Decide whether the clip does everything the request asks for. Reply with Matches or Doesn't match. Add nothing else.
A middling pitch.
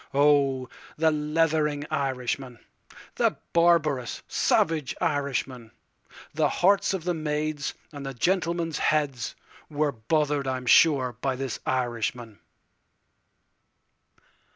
Matches